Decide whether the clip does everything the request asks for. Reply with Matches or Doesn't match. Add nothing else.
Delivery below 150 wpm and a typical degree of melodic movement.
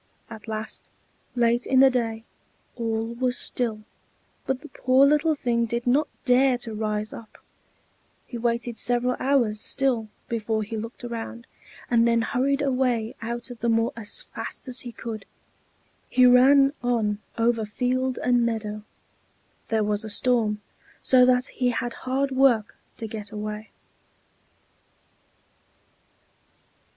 Doesn't match